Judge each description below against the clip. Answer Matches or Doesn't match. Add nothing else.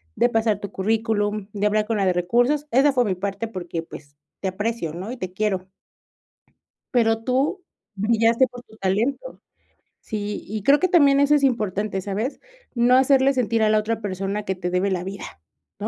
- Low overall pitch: Doesn't match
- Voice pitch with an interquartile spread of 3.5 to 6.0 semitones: Matches